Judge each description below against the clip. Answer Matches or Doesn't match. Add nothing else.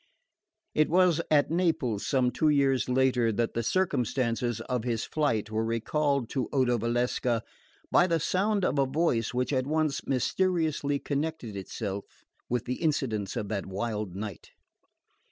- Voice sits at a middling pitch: Doesn't match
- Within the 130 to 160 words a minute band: Matches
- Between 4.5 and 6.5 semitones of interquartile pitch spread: Matches